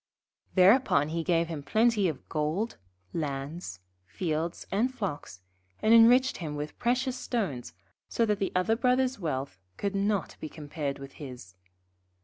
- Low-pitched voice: No, medium, 175 Hz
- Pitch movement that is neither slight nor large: No, wide, 7.3 semitones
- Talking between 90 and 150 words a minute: Yes, average, 140 wpm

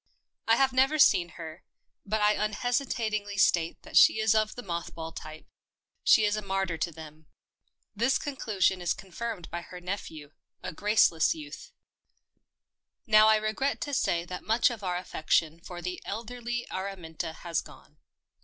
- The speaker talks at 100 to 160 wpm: No, average, 170 wpm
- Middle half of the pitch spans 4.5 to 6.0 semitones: Yes, average, 4.8 semitones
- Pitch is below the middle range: No, high, 200 Hz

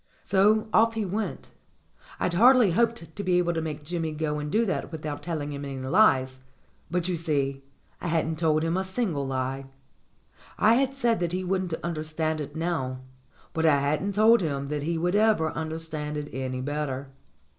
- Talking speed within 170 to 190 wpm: Yes, average, 185 wpm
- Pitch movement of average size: Yes, average, 4.3 semitones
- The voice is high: No, medium, 160 Hz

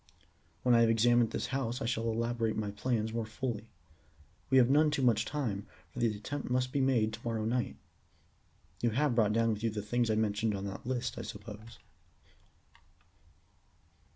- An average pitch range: No, narrow, 2.3 semitones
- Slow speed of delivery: No, average, 180 wpm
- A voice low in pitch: Yes, low, 115 Hz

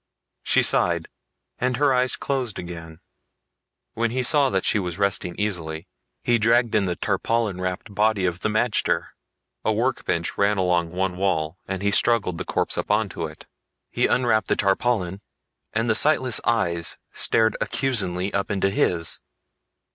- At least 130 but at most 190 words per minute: Yes, average, 155 wpm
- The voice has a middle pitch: No, low, 100 Hz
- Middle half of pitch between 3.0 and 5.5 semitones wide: Yes, average, 4.7 semitones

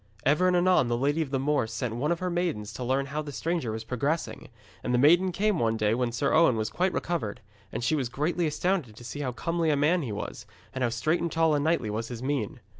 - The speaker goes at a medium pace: No, fast, 260 wpm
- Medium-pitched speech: Yes, medium, 145 Hz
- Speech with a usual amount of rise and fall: No, wide, 5.8 semitones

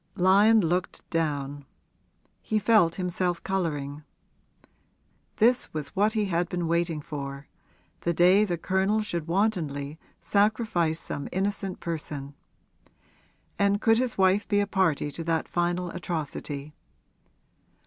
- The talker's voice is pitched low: No, medium, 175 Hz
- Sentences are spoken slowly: Yes, slow, 120 wpm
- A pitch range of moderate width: Yes, average, 4.2 semitones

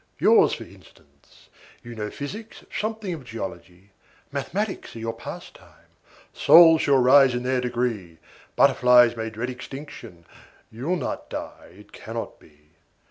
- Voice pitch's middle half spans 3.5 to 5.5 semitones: Yes, average, 4.3 semitones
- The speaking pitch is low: Yes, low, 125 Hz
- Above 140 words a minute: No, slow, 135 wpm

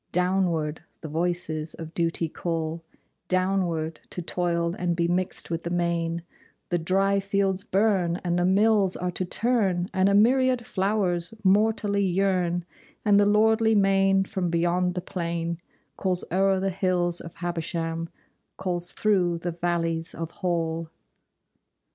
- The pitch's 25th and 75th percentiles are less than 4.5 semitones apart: Yes, narrow, 2.4 semitones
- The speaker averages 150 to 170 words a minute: No, average, 140 wpm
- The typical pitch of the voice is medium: Yes, medium, 180 Hz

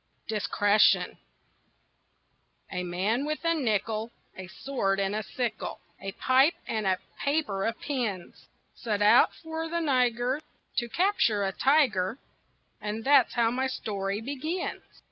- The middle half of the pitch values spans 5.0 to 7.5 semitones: Yes, average, 5.3 semitones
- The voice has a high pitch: Yes, high, 230 Hz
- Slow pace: Yes, slow, 130 wpm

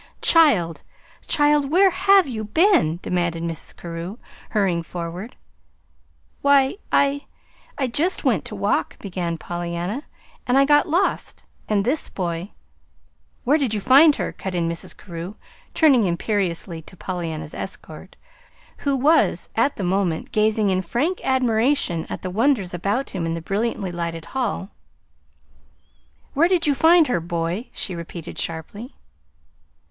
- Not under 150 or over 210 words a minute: No, average, 140 wpm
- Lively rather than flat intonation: Yes, wide, 8.4 semitones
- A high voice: Yes, high, 205 Hz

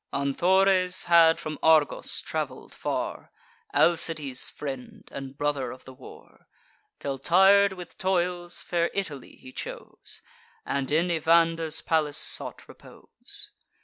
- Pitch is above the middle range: No, medium, 160 Hz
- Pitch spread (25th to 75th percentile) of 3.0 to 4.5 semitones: Yes, average, 3.9 semitones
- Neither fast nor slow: No, slow, 115 wpm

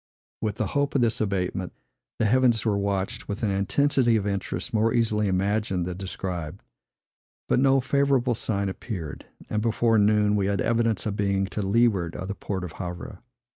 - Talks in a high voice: No, low, 105 Hz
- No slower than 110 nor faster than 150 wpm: No, average, 175 wpm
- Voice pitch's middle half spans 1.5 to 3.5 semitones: Yes, average, 3.1 semitones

